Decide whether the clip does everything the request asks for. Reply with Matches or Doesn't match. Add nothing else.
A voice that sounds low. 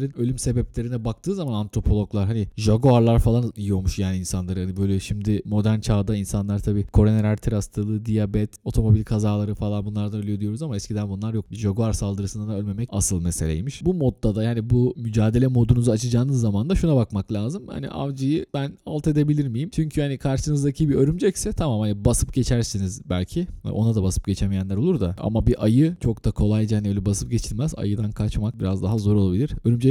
Matches